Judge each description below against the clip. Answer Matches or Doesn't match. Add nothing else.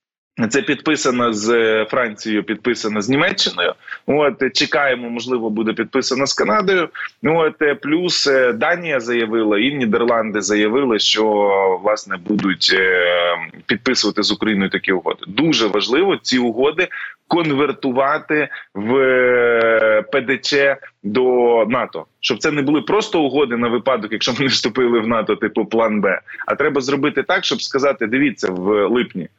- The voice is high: Doesn't match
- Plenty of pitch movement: Doesn't match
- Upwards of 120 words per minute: Matches